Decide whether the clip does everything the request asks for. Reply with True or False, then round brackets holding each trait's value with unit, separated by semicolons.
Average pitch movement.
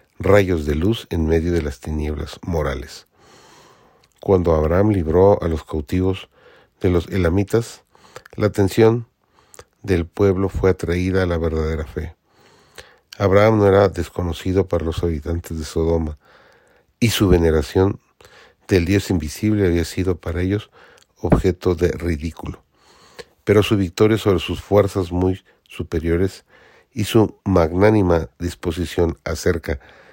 True (3.1 semitones)